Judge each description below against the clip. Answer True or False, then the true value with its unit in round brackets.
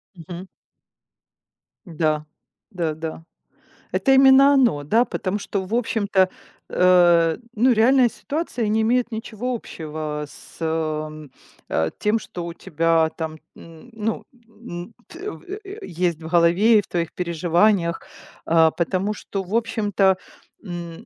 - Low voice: False (185 Hz)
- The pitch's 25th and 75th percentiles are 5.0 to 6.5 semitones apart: True (5.5 semitones)